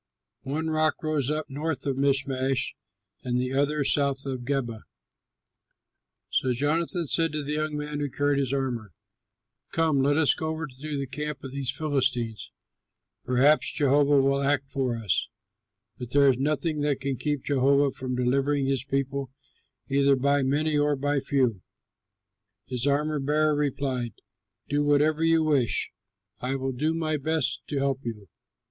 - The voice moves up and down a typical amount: No, narrow, 2.0 semitones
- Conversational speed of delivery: Yes, average, 160 wpm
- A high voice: No, medium, 140 Hz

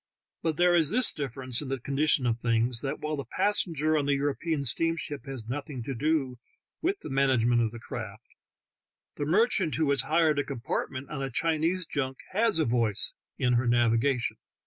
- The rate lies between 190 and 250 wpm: Yes, average, 195 wpm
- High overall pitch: No, medium, 140 Hz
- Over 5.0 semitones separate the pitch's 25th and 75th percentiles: No, average, 4.3 semitones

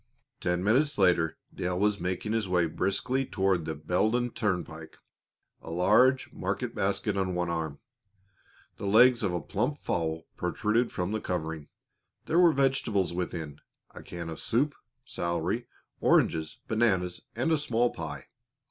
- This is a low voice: Yes, very low, 95 Hz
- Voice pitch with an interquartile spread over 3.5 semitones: Yes, average, 5.3 semitones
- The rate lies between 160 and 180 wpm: No, average, 145 wpm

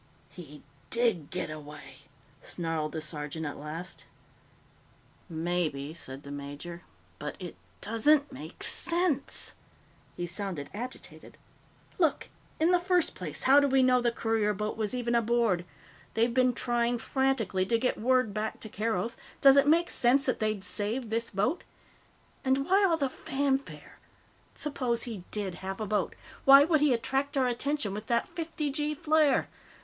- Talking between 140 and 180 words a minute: Yes, average, 155 wpm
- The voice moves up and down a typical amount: No, wide, 6.8 semitones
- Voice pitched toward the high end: Yes, high, 235 Hz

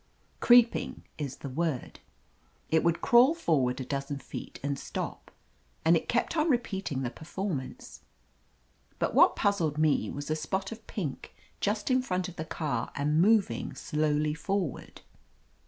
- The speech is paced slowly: No, average, 155 wpm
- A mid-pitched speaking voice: Yes, medium, 160 Hz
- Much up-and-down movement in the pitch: Yes, wide, 6.0 semitones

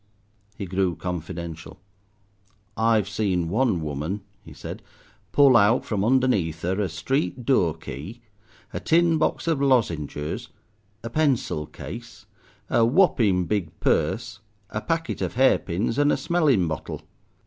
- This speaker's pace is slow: Yes, slow, 130 wpm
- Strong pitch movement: Yes, wide, 7.3 semitones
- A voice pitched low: Yes, low, 105 Hz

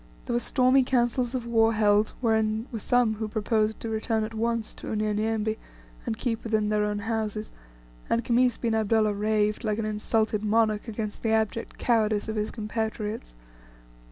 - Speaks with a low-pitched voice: No, high, 220 Hz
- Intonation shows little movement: Yes, narrow, 1.3 semitones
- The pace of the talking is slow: No, average, 170 wpm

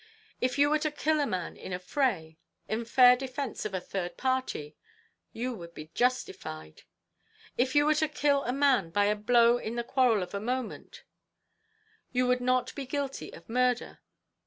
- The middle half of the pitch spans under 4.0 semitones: No, average, 4.7 semitones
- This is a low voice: No, very high, 250 Hz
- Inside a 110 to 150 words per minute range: No, average, 185 wpm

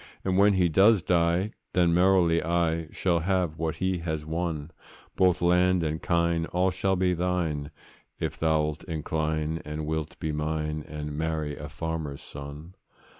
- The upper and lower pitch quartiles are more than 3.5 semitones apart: No, narrow, 2.5 semitones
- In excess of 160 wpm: No, average, 155 wpm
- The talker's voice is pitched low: Yes, very low, 80 Hz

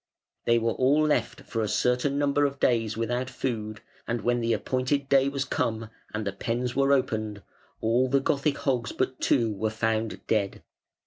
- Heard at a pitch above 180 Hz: No, low, 120 Hz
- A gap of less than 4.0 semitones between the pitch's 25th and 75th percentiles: Yes, average, 3.4 semitones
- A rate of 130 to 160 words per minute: No, average, 180 wpm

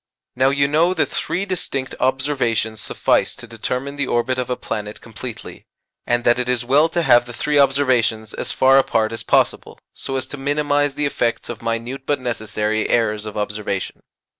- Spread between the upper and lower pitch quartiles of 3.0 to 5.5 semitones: Yes, average, 3.6 semitones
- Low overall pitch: Yes, low, 125 Hz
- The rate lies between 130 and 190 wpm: Yes, average, 185 wpm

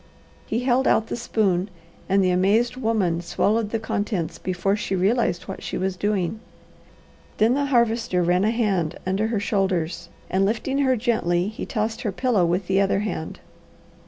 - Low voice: No, high, 205 Hz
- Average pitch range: Yes, average, 3.6 semitones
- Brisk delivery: No, average, 170 wpm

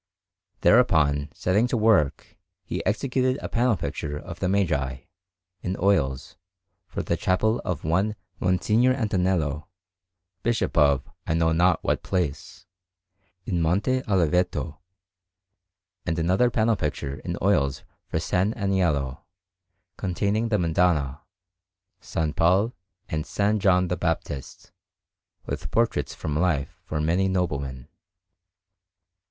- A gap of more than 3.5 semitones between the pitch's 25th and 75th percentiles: Yes, average, 5.0 semitones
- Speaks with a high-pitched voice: No, very low, 90 Hz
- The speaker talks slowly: Yes, slow, 115 wpm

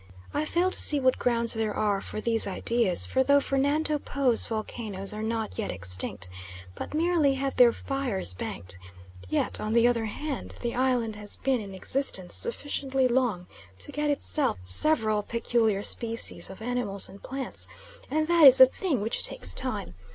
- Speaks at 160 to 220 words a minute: Yes, average, 170 wpm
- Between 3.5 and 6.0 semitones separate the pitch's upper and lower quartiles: Yes, average, 4.7 semitones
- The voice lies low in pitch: No, high, 235 Hz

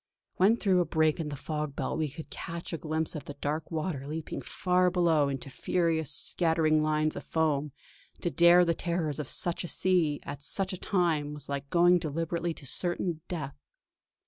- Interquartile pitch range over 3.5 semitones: No, narrow, 2.6 semitones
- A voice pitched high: No, medium, 160 Hz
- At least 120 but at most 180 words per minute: No, average, 190 wpm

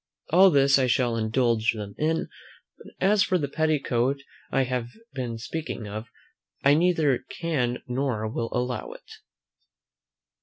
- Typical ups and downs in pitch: Yes, average, 4.8 semitones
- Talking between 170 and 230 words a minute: No, average, 140 wpm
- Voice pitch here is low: Yes, low, 130 Hz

